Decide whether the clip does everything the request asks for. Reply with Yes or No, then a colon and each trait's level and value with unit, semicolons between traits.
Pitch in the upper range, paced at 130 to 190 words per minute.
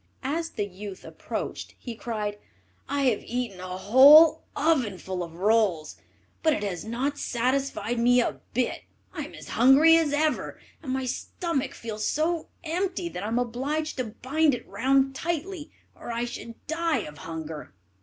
Yes: very high, 250 Hz; average, 165 wpm